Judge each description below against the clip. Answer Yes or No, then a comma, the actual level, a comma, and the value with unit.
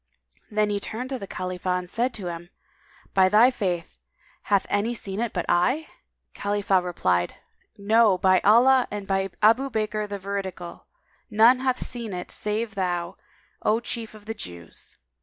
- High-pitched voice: Yes, high, 205 Hz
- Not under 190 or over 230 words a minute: No, average, 160 wpm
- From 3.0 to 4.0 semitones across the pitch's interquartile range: Yes, average, 3.5 semitones